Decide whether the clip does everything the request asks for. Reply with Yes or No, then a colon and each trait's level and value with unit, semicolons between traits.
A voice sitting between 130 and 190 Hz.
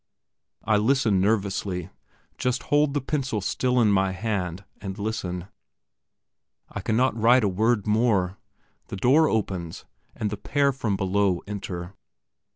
No: low, 105 Hz